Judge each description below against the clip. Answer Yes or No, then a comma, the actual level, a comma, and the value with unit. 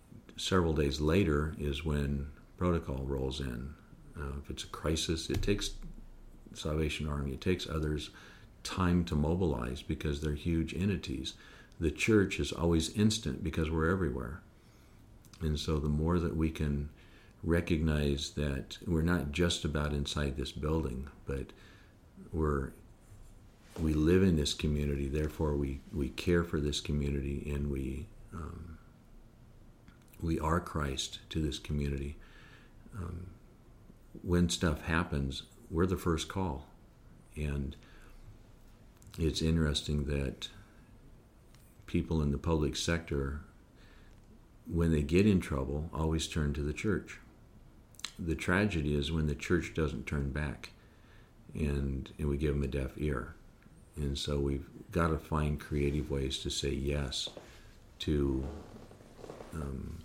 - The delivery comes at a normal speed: No, slow, 130 wpm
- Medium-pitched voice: No, very low, 80 Hz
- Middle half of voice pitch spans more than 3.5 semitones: Yes, average, 4.2 semitones